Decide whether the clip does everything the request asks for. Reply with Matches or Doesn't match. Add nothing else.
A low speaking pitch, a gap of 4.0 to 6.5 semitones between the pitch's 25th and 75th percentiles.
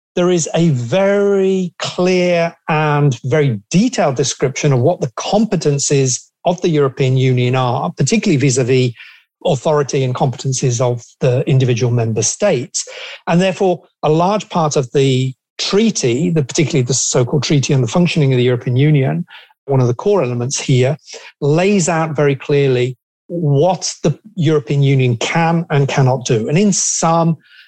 Doesn't match